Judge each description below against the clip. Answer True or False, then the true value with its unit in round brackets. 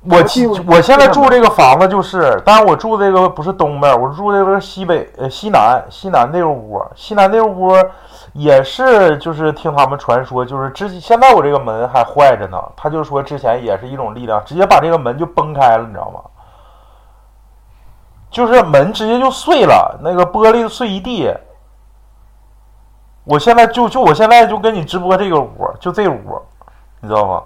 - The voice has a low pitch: False (185 Hz)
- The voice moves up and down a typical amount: False (7.7 semitones)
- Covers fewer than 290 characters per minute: True (275 characters per minute)